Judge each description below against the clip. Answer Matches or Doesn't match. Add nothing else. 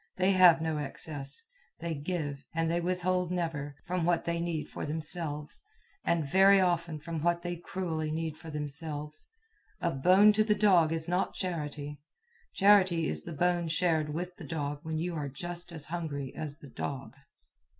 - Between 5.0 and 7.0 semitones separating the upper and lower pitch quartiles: Doesn't match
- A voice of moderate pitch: Matches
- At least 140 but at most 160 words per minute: Doesn't match